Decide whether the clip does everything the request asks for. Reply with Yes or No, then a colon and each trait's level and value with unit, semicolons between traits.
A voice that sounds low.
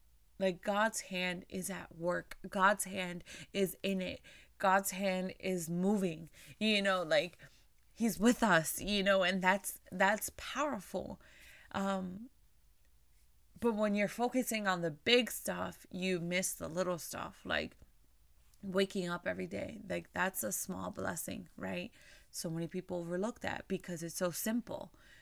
No: high, 190 Hz